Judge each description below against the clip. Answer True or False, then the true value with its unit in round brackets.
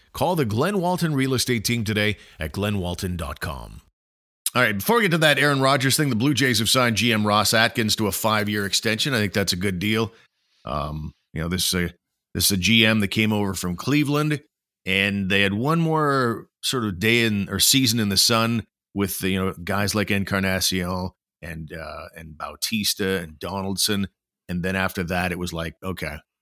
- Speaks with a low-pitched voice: True (100 Hz)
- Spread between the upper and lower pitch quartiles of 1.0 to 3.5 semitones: False (3.9 semitones)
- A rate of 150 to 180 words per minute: False (200 wpm)